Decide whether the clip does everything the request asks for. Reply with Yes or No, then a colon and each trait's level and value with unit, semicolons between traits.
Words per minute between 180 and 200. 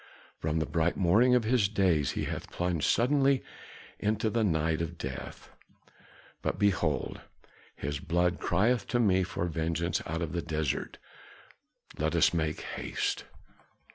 No: average, 145 wpm